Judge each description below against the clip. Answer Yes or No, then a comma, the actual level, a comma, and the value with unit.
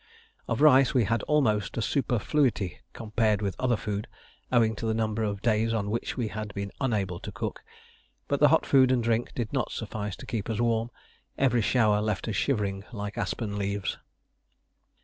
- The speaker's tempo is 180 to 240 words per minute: Yes, average, 185 wpm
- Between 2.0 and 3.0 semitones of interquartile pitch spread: Yes, narrow, 2.5 semitones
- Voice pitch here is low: Yes, low, 110 Hz